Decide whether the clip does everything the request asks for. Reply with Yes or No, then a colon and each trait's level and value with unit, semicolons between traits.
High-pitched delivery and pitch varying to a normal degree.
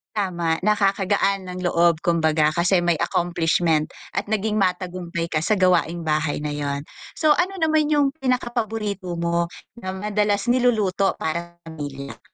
No: medium, 180 Hz; average, 4.0 semitones